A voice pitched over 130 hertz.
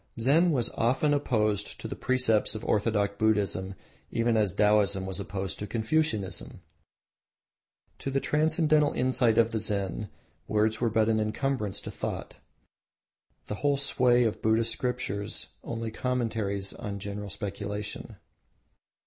No: low, 110 Hz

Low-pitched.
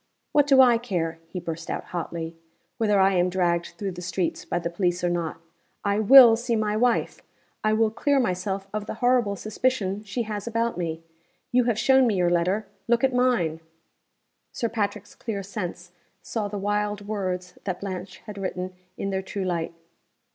No: high, 200 Hz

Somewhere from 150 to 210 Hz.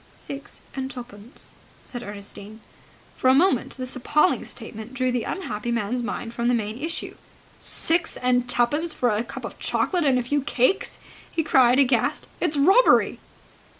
No: very high, 250 Hz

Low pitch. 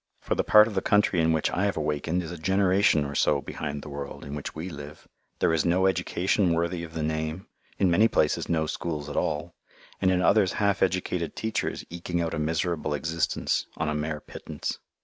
Yes: very low, 85 Hz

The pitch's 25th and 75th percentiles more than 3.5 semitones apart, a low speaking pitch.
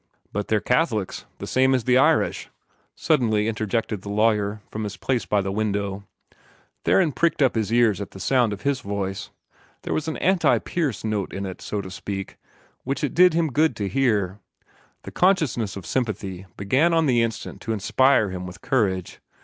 Yes: average, 4.8 semitones; low, 110 Hz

